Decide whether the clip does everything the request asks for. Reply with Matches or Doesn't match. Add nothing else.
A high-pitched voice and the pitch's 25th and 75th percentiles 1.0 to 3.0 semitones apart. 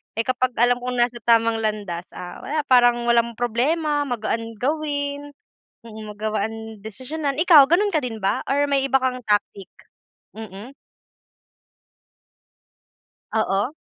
Doesn't match